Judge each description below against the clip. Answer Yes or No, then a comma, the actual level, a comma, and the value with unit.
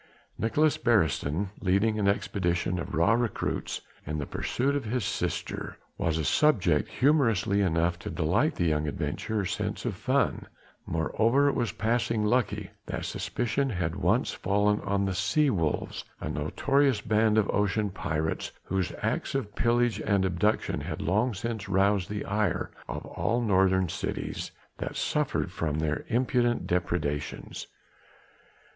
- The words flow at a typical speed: Yes, average, 145 wpm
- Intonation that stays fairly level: No, average, 4.9 semitones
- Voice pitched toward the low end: Yes, low, 100 Hz